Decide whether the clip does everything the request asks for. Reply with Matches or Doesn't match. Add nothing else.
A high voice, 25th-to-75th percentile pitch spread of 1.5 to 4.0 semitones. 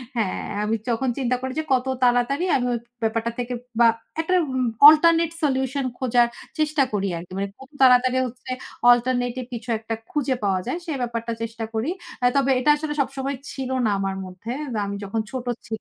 Matches